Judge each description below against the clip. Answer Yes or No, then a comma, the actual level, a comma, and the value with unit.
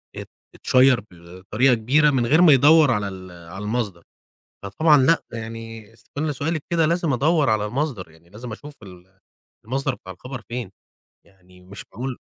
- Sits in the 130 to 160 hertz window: No, low, 120 Hz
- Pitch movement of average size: No, wide, 6.6 semitones